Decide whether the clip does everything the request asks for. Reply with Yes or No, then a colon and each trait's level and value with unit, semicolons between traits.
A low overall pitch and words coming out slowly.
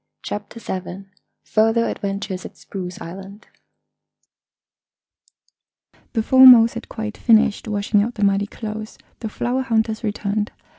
No: high, 215 Hz; slow, 115 wpm